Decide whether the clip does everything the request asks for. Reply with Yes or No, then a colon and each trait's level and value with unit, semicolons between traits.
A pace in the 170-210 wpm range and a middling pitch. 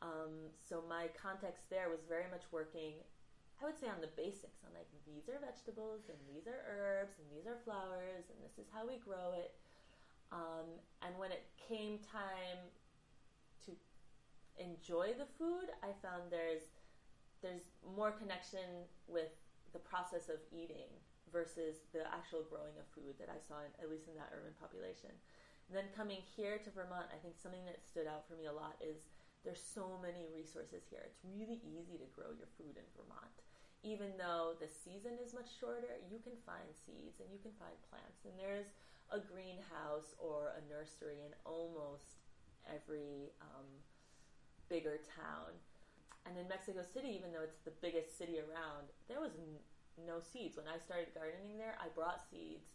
Yes: average, 175 wpm; medium, 170 Hz